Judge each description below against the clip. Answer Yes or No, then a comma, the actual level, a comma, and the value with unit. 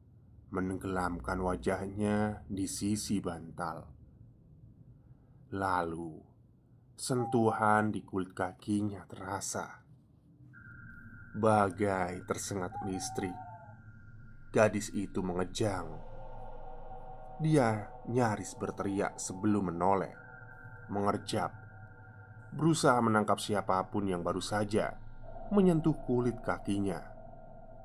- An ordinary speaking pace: No, slow, 70 wpm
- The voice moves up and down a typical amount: Yes, average, 4.2 semitones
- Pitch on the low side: Yes, low, 105 Hz